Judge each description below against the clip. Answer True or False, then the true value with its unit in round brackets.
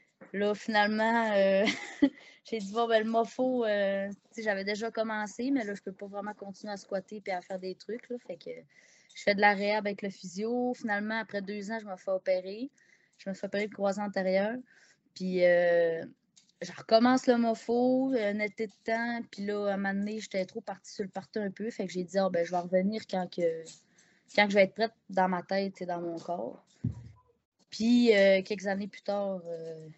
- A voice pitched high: True (205 Hz)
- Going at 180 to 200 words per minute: False (215 wpm)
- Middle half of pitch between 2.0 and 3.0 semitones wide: True (2.7 semitones)